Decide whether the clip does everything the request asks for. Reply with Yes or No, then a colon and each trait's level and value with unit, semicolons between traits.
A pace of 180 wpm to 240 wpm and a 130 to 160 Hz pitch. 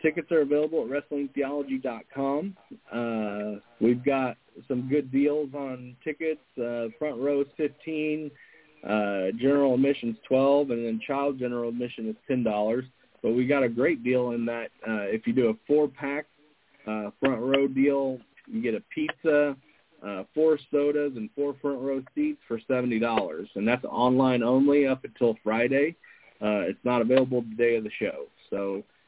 No: average, 165 wpm; low, 135 Hz